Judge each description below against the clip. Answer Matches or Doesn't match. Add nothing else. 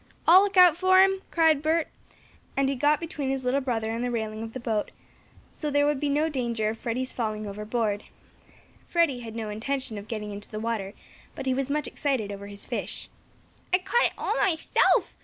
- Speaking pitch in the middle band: Doesn't match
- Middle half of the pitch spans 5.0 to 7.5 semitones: Matches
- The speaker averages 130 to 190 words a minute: Doesn't match